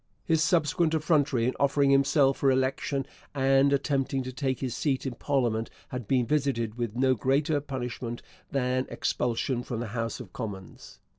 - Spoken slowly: No, average, 160 wpm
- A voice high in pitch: No, low, 130 Hz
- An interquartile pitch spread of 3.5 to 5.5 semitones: No, narrow, 2.5 semitones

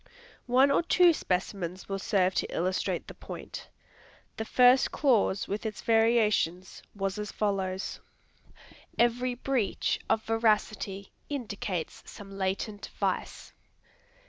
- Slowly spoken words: Yes, slow, 115 wpm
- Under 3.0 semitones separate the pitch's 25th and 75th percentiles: No, average, 3.7 semitones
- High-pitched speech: Yes, high, 210 Hz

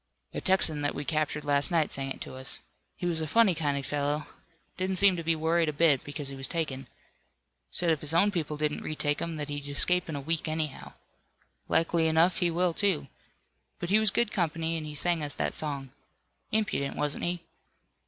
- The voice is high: No, medium, 160 Hz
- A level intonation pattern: No, average, 3.0 semitones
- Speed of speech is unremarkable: No, fast, 210 wpm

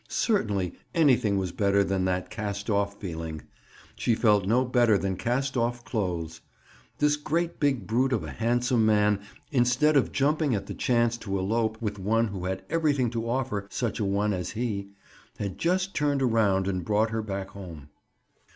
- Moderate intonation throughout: Yes, average, 4.1 semitones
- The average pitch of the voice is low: Yes, low, 110 Hz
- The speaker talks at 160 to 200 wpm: Yes, average, 175 wpm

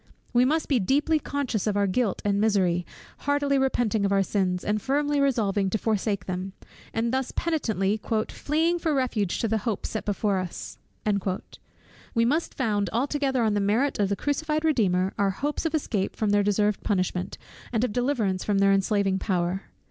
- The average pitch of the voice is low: No, high, 215 Hz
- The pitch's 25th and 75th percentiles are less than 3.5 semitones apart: No, wide, 5.4 semitones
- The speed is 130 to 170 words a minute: No, average, 180 wpm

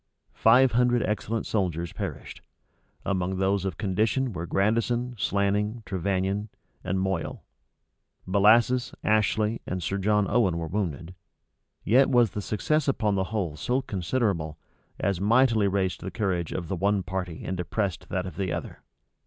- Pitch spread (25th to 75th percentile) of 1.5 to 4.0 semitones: Yes, average, 3.3 semitones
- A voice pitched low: Yes, low, 100 Hz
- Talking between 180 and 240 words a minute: No, average, 145 wpm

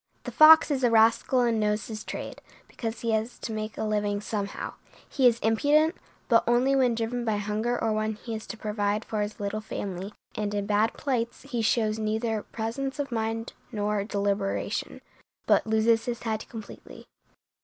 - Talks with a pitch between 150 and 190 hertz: No, high, 220 Hz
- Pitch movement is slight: Yes, narrow, 2.0 semitones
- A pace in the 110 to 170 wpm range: No, average, 180 wpm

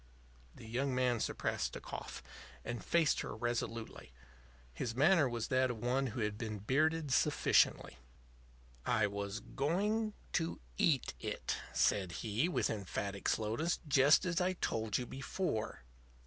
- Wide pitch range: Yes, wide, 6.0 semitones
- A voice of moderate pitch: No, low, 125 Hz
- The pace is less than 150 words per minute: Yes, average, 140 wpm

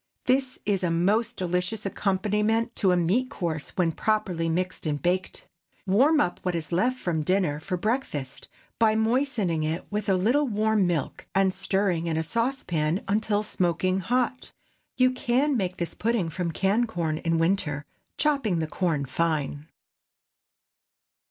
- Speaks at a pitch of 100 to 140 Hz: No, high, 190 Hz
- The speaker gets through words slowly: No, average, 150 wpm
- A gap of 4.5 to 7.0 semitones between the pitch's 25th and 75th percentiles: Yes, average, 5.0 semitones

